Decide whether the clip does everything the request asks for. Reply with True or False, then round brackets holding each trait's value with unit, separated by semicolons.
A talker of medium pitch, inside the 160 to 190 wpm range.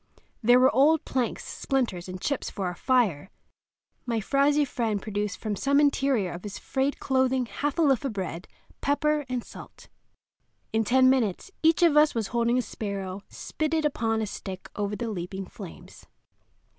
False (240 Hz; 170 wpm)